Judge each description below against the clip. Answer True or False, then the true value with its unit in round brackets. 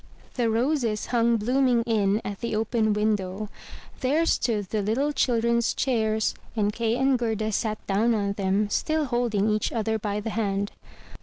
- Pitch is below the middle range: False (220 Hz)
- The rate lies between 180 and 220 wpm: False (160 wpm)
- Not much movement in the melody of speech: True (2.3 semitones)